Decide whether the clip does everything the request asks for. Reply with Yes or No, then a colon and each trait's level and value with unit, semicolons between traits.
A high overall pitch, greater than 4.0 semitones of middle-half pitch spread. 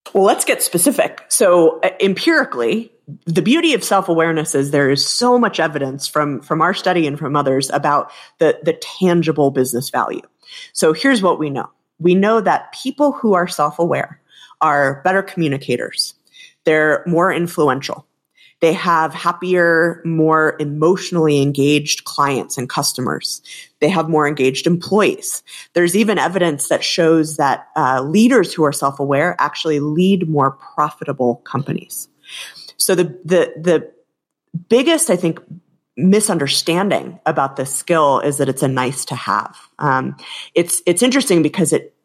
No: medium, 165 Hz; average, 4.5 semitones